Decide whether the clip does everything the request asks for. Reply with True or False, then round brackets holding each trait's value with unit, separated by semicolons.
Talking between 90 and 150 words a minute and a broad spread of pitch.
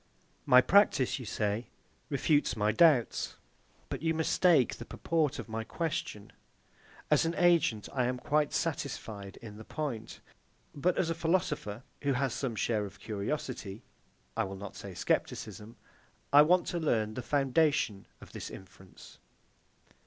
True (145 wpm; 6.4 semitones)